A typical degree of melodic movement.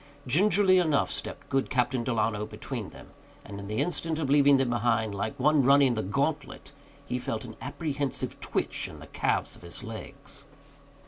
Yes: average, 4.4 semitones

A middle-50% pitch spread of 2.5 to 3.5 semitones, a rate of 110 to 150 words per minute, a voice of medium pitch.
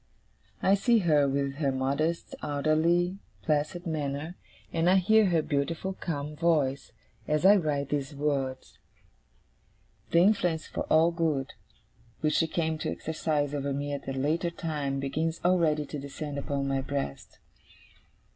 Yes: average, 3.0 semitones; average, 145 wpm; medium, 150 Hz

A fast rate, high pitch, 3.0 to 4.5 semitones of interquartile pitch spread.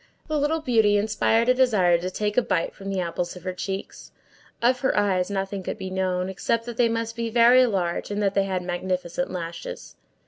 Yes: fast, 210 wpm; high, 200 Hz; average, 4.1 semitones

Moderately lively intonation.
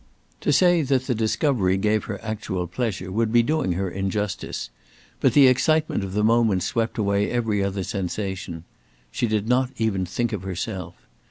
Yes: average, 3.8 semitones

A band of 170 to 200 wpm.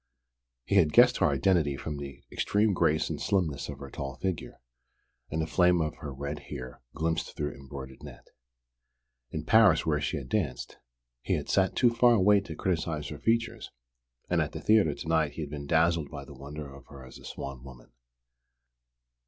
Yes: average, 185 wpm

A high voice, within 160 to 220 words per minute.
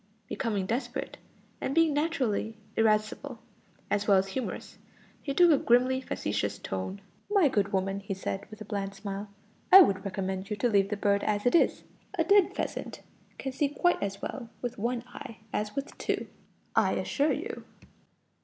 Yes: high, 215 Hz; average, 175 wpm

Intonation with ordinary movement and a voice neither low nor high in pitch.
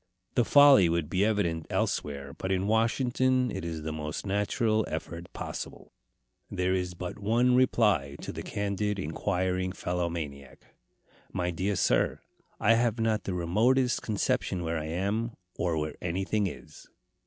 No: average, 4.6 semitones; very low, 95 Hz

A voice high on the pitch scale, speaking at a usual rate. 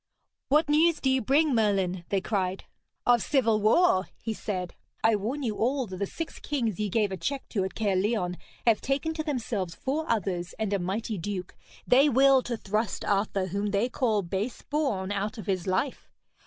Yes: high, 215 Hz; average, 190 wpm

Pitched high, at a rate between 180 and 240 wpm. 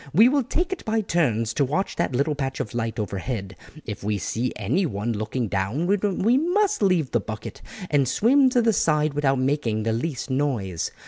No: medium, 140 Hz; average, 190 wpm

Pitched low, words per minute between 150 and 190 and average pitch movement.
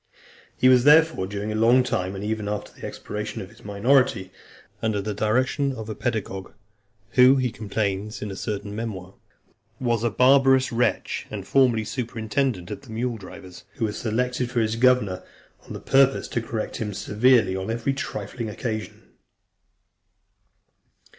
Yes: low, 110 Hz; average, 155 wpm; average, 3.4 semitones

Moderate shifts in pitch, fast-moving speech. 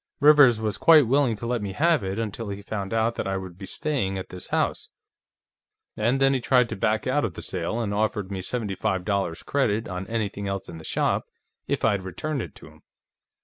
Yes: average, 4.2 semitones; fast, 225 wpm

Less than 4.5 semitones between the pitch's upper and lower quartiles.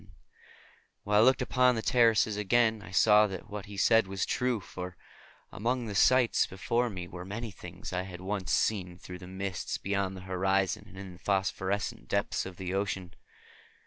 Yes: average, 2.9 semitones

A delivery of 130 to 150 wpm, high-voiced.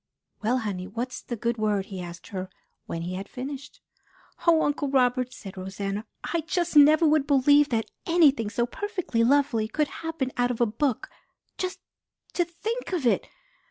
No: average, 170 wpm; very high, 255 Hz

